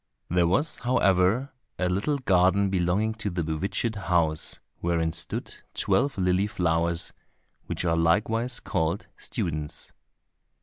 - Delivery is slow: Yes, slow, 120 wpm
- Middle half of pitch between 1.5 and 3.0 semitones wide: No, average, 4.0 semitones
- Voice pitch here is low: Yes, very low, 90 Hz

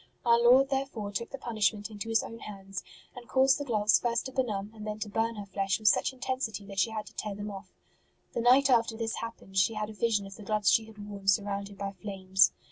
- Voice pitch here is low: No, high, 215 Hz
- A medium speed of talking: No, fast, 240 wpm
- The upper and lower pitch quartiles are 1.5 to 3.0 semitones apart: Yes, average, 2.7 semitones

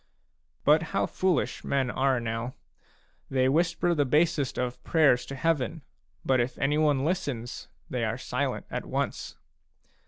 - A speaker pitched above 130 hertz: Yes, medium, 140 Hz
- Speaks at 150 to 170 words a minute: No, slow, 135 wpm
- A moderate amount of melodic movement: Yes, average, 4.1 semitones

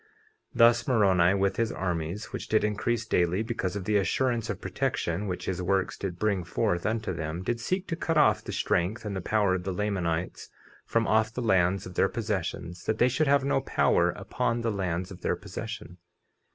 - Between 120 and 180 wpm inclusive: No, fast, 205 wpm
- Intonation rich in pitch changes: No, average, 4.0 semitones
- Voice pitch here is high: No, low, 100 Hz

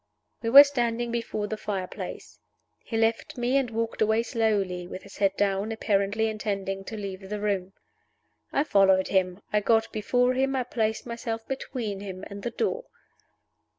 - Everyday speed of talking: Yes, average, 170 wpm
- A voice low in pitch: No, high, 220 Hz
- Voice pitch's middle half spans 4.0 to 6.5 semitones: No, average, 3.0 semitones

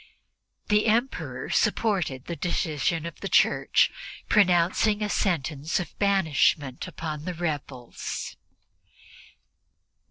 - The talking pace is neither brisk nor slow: No, slow, 95 wpm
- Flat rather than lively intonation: No, average, 5.0 semitones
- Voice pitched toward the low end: No, medium, 170 Hz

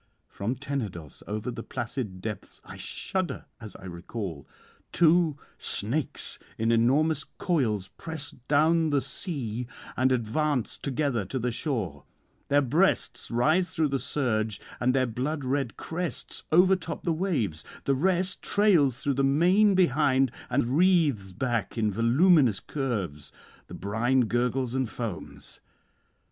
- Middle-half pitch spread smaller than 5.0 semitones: No, wide, 5.5 semitones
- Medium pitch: No, low, 130 Hz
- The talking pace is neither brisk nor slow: No, slow, 130 wpm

